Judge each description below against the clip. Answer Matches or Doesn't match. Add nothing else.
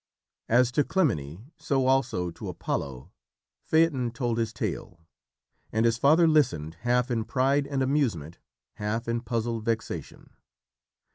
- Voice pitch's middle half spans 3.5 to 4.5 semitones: Matches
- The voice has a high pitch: Doesn't match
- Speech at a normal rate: Doesn't match